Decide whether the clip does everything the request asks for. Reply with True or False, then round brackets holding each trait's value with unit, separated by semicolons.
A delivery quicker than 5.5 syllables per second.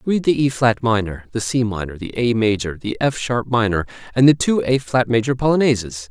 False (5.4 syllables/s)